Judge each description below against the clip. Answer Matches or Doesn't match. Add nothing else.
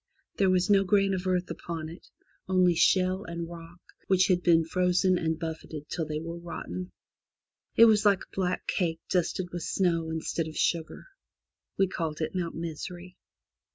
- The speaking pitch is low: Doesn't match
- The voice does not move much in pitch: Matches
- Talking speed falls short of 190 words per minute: Matches